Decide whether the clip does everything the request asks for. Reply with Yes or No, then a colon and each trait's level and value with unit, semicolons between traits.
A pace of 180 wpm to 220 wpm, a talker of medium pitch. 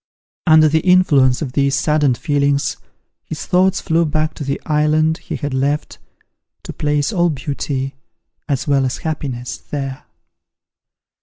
No: average, 145 wpm; medium, 150 Hz